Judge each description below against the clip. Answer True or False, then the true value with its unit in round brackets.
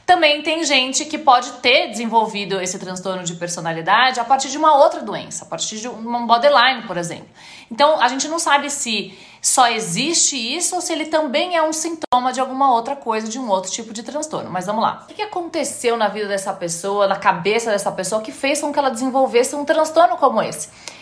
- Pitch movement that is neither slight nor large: False (6.3 semitones)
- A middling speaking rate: False (210 wpm)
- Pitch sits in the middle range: False (255 Hz)